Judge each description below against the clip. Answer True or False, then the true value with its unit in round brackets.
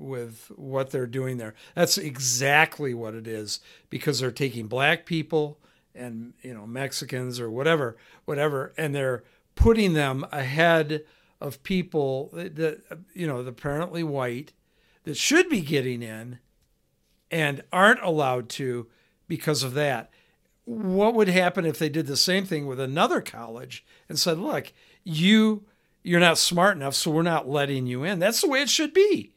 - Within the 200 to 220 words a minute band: False (160 wpm)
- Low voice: False (150 Hz)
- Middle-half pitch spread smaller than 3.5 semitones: False (4.8 semitones)